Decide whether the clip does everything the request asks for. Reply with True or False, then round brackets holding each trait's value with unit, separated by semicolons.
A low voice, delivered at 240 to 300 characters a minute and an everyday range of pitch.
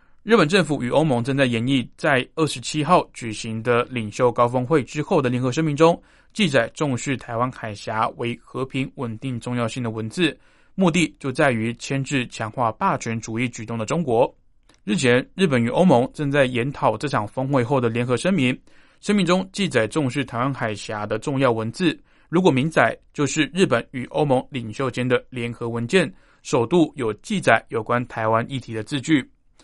True (130 Hz; 280 characters per minute; 4.2 semitones)